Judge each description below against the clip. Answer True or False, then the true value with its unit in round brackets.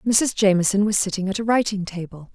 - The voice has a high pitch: True (200 Hz)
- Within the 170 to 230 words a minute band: True (205 wpm)